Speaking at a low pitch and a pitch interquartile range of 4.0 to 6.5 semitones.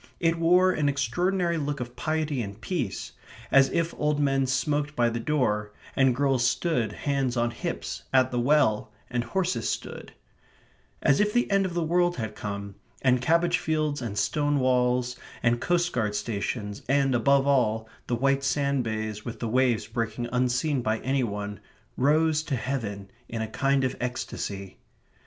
Yes: low, 130 Hz; average, 4.4 semitones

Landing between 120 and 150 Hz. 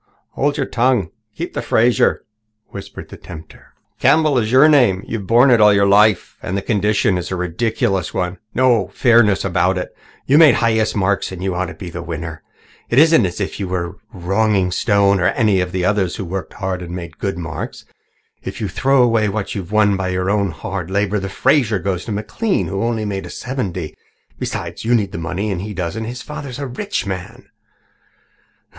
No: low, 100 Hz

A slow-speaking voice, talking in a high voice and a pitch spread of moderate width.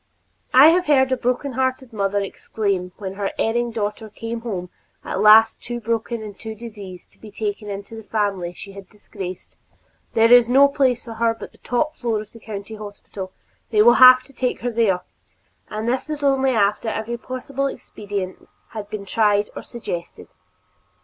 No: average, 175 wpm; high, 220 Hz; average, 3.2 semitones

